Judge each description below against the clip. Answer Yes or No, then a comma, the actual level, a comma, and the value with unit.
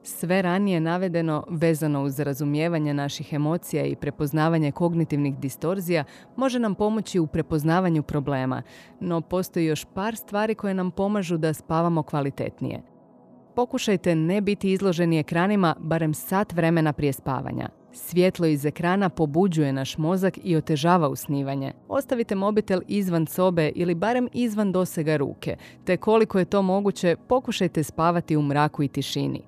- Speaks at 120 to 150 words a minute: Yes, average, 140 wpm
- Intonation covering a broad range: No, average, 3.9 semitones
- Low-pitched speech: No, medium, 170 Hz